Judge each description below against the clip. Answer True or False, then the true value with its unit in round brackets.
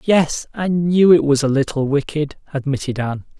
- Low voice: False (150 Hz)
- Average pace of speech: True (175 wpm)